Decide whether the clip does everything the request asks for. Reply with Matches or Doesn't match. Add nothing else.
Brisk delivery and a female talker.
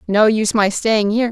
Matches